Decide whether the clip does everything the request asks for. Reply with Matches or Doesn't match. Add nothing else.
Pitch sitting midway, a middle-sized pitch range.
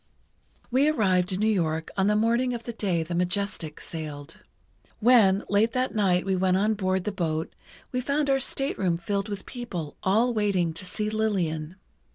Doesn't match